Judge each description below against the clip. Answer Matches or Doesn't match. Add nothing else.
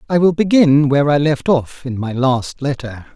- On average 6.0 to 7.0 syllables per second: Doesn't match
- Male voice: Matches